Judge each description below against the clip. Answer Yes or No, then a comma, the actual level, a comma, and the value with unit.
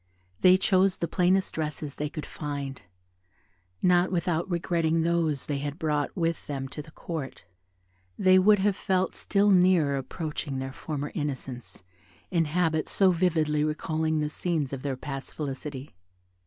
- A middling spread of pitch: Yes, average, 3.6 semitones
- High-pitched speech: No, medium, 155 Hz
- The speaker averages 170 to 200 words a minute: No, average, 150 wpm